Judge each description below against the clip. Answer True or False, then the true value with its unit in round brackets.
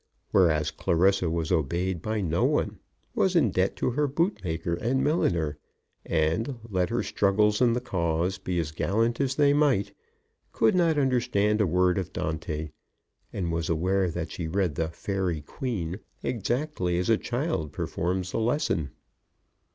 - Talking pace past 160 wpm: False (155 wpm)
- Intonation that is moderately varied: False (6.1 semitones)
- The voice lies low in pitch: True (95 Hz)